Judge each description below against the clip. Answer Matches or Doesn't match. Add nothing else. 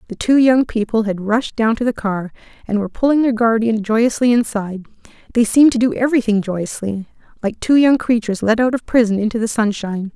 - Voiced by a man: Doesn't match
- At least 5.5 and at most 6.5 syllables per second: Matches